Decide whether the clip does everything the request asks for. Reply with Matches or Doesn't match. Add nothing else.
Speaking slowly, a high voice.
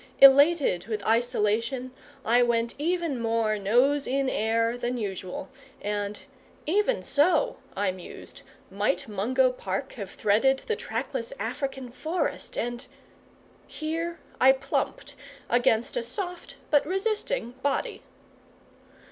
Matches